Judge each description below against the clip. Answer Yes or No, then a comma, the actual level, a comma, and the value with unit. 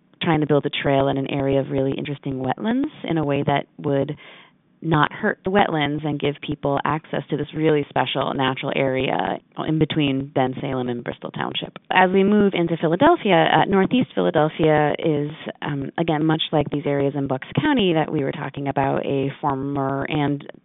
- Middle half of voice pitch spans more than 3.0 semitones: No, narrow, 2.4 semitones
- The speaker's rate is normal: Yes, average, 185 wpm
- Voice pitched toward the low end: No, medium, 145 Hz